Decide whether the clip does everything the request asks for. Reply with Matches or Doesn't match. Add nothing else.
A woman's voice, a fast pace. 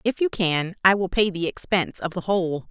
Matches